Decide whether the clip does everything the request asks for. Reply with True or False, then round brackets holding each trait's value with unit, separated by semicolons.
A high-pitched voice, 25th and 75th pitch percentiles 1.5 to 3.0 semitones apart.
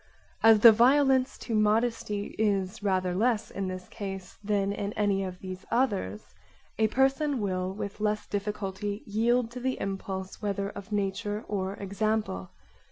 True (205 Hz; 2.5 semitones)